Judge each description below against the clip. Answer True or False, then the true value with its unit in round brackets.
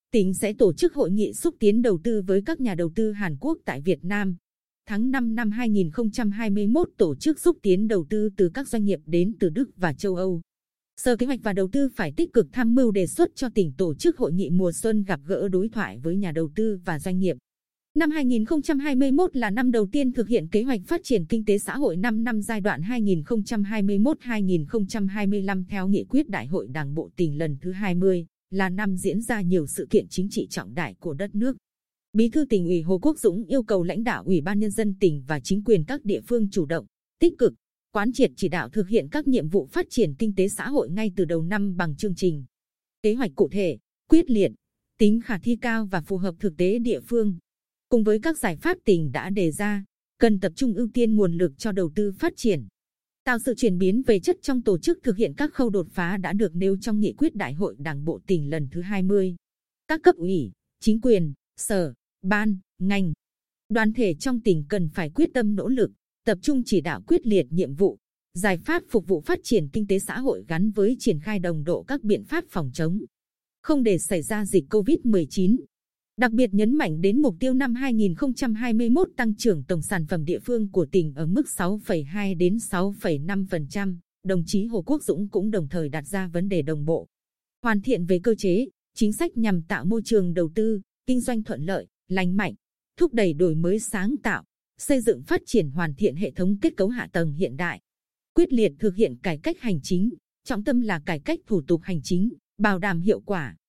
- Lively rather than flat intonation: False (4.4 semitones)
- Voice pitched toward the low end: False (205 Hz)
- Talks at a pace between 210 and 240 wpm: True (220 wpm)